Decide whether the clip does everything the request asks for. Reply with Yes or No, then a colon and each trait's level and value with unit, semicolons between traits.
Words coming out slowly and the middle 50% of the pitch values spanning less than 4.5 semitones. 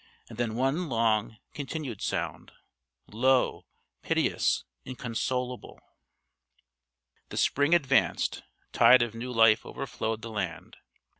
Yes: slow, 105 wpm; average, 2.9 semitones